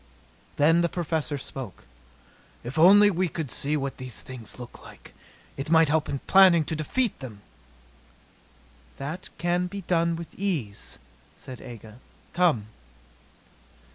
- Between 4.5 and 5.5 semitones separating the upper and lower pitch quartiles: Yes, average, 5.1 semitones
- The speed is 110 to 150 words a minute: Yes, slow, 135 wpm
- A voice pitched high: No, medium, 155 Hz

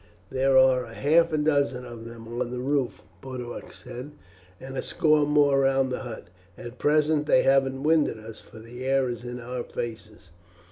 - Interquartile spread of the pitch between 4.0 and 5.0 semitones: No, average, 2.9 semitones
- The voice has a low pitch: Yes, low, 130 Hz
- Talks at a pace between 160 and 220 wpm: Yes, average, 185 wpm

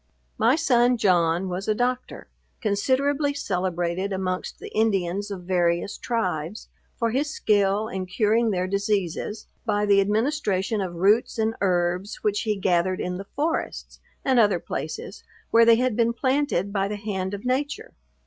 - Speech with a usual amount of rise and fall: Yes, average, 3.9 semitones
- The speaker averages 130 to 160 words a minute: Yes, average, 155 wpm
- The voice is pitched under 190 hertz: No, high, 205 Hz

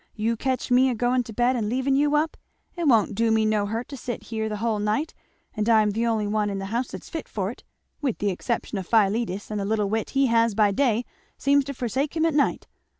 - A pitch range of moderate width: Yes, average, 3.6 semitones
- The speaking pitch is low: No, high, 230 Hz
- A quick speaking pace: Yes, fast, 250 wpm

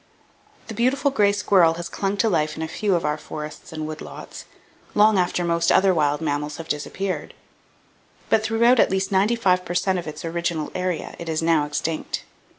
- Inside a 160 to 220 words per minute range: Yes, average, 195 wpm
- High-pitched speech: No, medium, 175 Hz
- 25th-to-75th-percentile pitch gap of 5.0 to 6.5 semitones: No, average, 4.0 semitones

